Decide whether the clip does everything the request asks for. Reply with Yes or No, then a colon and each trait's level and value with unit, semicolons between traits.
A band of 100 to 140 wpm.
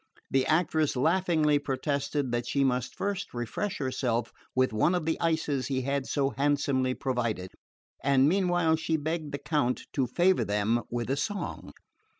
No: average, 155 wpm